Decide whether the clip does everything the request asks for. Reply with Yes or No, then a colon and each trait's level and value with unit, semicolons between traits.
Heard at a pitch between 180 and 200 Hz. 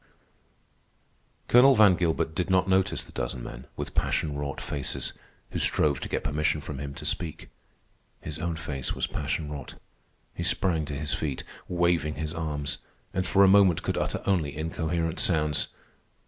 No: very low, 80 Hz